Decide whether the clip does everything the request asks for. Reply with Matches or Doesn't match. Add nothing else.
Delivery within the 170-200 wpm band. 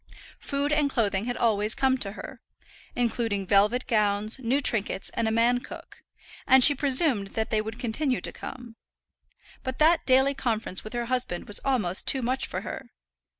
Matches